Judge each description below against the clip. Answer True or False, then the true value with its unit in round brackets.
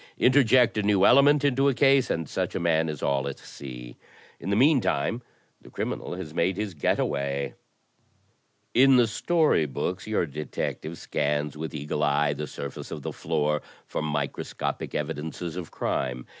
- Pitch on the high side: False (80 Hz)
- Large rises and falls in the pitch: True (7.9 semitones)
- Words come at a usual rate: True (170 wpm)